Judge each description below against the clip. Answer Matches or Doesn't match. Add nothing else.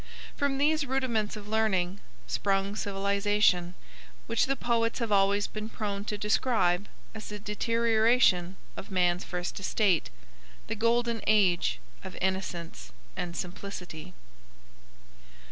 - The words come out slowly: Matches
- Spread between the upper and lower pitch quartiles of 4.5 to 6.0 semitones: Doesn't match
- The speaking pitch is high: Matches